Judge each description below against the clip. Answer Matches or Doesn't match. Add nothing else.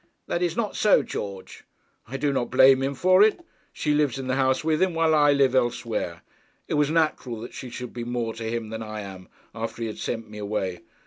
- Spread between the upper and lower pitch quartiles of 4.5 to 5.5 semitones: Matches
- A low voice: Matches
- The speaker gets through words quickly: Matches